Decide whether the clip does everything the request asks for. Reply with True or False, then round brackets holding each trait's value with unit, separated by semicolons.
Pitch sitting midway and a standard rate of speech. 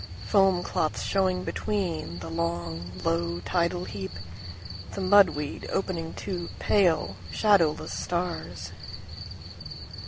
False (155 Hz; 90 wpm)